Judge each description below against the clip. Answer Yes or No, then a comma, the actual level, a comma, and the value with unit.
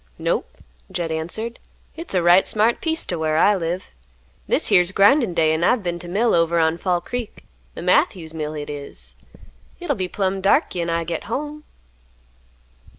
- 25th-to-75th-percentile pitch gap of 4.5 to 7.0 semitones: Yes, average, 5.0 semitones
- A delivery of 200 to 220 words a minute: No, average, 175 wpm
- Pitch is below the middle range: No, medium, 180 Hz